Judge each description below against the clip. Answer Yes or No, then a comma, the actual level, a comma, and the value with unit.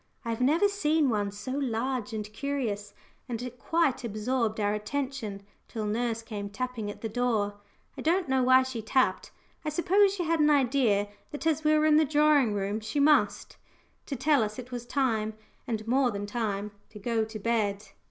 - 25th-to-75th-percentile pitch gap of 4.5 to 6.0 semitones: Yes, average, 5.0 semitones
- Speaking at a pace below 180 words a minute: No, average, 190 wpm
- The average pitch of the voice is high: Yes, high, 240 Hz